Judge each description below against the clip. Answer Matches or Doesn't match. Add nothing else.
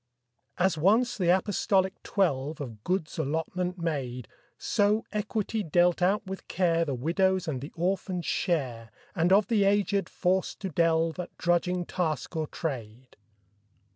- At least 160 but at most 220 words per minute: Doesn't match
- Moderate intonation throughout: Matches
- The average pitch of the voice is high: Doesn't match